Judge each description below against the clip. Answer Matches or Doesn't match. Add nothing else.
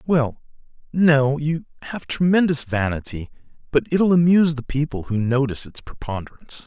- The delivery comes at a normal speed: Doesn't match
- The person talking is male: Matches